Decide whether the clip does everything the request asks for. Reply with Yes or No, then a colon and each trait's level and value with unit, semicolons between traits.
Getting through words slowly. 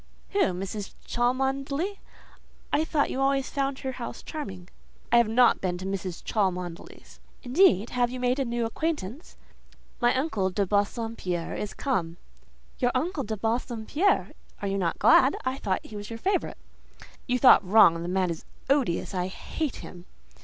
No: average, 155 wpm